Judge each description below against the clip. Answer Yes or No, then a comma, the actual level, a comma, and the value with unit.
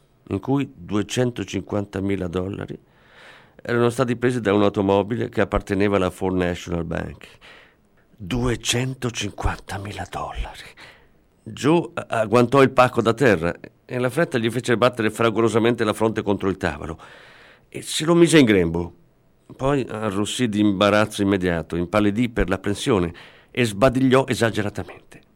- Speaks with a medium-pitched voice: No, low, 105 Hz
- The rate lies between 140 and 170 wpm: No, average, 125 wpm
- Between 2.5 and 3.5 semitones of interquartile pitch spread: No, average, 4.1 semitones